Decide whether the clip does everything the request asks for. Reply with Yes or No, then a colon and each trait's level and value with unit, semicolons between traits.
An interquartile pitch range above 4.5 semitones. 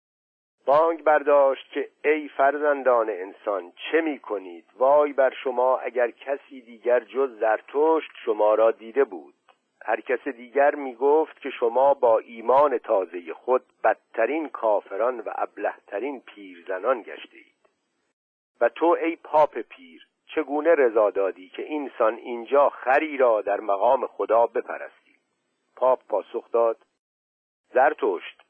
Yes: average, 5.1 semitones